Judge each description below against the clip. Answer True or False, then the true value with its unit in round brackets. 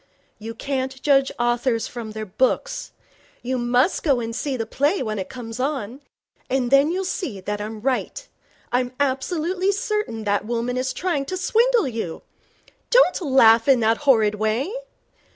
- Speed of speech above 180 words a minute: False (150 wpm)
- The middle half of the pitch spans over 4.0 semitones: True (4.5 semitones)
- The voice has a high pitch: True (255 Hz)